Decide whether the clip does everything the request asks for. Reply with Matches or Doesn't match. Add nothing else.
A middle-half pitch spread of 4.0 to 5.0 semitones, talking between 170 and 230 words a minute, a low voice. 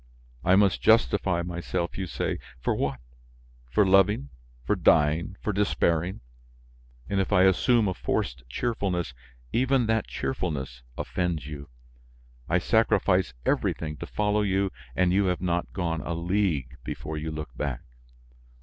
Doesn't match